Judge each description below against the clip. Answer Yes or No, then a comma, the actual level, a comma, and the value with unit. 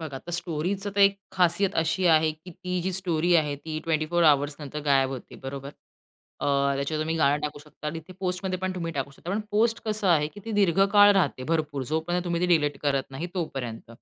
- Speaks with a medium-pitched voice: Yes, medium, 165 Hz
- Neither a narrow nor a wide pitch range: Yes, average, 3.9 semitones